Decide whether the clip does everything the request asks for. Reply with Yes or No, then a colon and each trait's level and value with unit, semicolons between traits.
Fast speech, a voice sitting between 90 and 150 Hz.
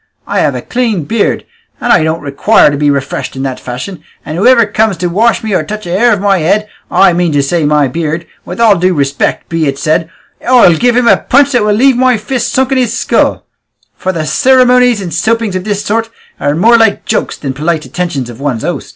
No: fast, 230 wpm; high, 190 Hz